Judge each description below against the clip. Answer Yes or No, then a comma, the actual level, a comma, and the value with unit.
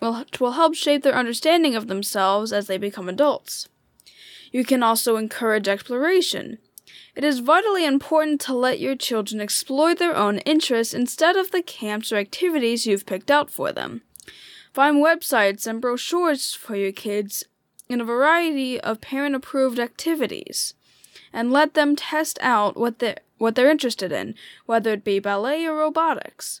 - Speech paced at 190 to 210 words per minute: No, average, 160 wpm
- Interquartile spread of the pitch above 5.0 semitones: Yes, wide, 5.6 semitones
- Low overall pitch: No, very high, 255 Hz